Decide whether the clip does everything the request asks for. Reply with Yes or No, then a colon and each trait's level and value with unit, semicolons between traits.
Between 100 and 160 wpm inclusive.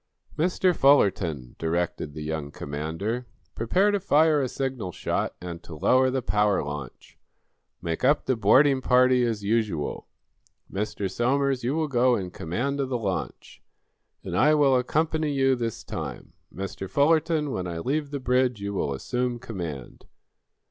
Yes: average, 155 wpm